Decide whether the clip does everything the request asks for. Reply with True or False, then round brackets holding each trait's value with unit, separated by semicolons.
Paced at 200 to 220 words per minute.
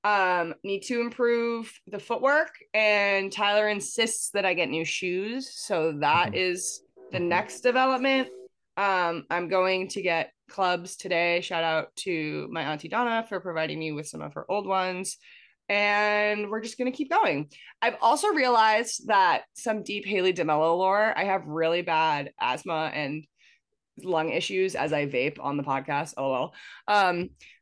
False (160 wpm)